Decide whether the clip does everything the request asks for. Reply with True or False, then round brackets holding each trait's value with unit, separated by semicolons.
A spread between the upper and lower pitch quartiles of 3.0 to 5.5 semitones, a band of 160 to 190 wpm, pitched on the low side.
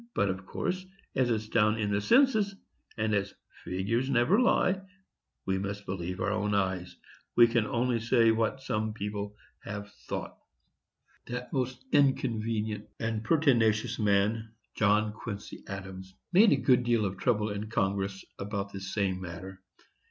False (3.3 semitones; 150 wpm; 110 Hz)